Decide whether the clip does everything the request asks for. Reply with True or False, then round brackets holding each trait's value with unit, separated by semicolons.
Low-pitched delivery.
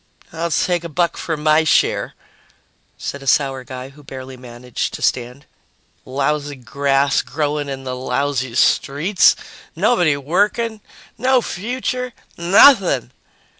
False (145 Hz)